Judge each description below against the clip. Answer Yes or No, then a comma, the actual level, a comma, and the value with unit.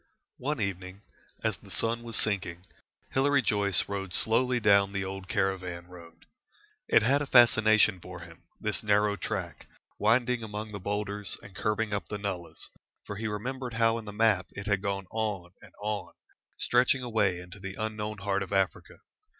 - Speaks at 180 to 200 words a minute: No, average, 170 wpm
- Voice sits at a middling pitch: No, low, 105 Hz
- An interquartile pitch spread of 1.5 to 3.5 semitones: Yes, narrow, 2.6 semitones